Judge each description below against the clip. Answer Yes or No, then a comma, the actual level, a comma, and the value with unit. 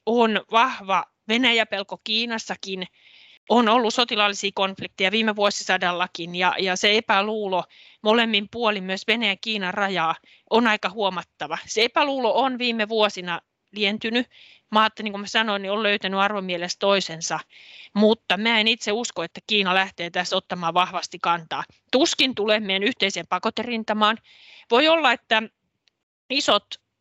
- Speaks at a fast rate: No, average, 135 wpm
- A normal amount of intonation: Yes, average, 3.1 semitones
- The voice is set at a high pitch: Yes, high, 210 Hz